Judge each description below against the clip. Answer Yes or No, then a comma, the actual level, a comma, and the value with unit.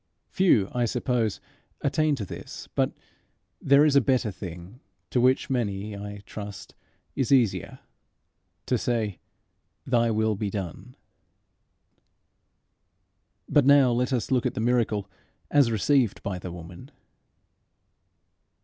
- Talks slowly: Yes, slow, 120 wpm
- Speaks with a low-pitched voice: Yes, low, 115 Hz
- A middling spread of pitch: Yes, average, 4.3 semitones